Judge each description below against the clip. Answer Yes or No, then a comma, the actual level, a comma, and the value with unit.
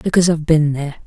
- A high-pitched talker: No, medium, 155 Hz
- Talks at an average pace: No, fast, 225 wpm